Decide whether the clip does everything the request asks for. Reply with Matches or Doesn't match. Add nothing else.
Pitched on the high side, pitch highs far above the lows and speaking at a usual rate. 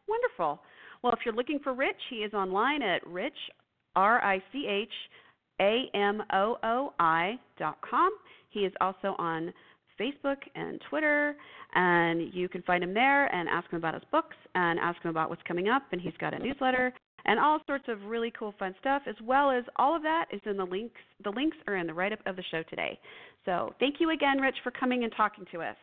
Matches